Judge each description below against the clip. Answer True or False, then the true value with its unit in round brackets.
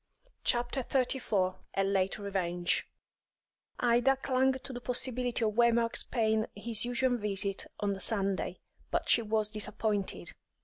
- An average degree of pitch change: True (3.6 semitones)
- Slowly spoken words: True (130 wpm)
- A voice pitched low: False (220 Hz)